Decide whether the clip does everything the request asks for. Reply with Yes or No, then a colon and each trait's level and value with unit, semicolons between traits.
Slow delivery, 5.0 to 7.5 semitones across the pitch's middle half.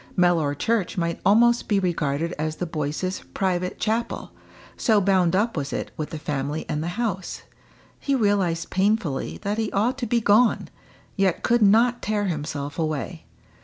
No: average, 165 wpm; average, 5.3 semitones